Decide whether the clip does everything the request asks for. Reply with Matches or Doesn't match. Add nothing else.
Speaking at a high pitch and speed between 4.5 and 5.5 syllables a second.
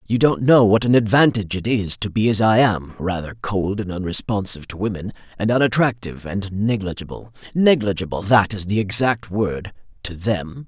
Doesn't match